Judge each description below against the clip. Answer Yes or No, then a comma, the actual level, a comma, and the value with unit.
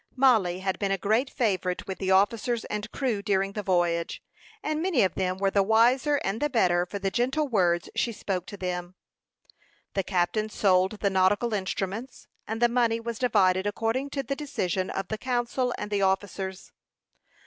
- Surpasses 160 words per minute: Yes, average, 180 wpm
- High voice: Yes, high, 205 Hz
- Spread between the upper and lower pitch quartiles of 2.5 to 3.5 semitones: No, average, 4.0 semitones